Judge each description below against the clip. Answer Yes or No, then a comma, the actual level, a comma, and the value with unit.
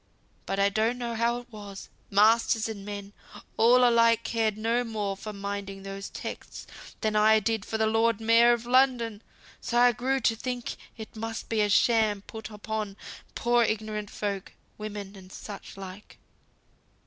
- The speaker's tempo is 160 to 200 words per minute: Yes, average, 165 wpm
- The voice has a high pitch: Yes, high, 220 Hz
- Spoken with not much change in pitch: Yes, narrow, 2.2 semitones